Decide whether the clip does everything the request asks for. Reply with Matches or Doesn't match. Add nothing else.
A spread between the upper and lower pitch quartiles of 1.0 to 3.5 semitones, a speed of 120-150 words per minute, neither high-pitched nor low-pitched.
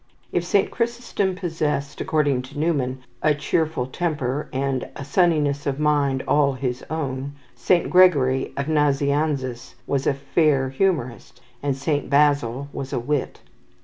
Matches